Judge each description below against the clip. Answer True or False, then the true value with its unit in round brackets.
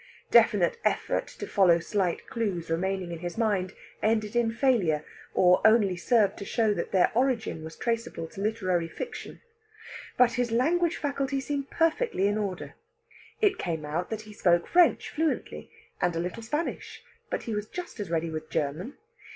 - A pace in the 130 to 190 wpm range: True (165 wpm)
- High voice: True (210 Hz)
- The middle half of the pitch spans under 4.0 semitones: False (5.5 semitones)